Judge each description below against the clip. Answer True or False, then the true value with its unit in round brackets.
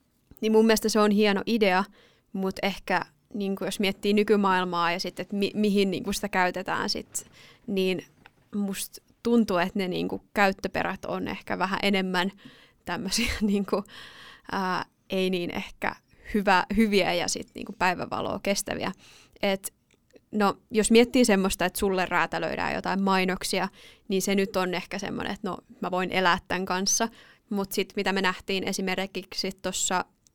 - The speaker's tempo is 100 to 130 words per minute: False (150 wpm)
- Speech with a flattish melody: True (2.1 semitones)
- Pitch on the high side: True (195 Hz)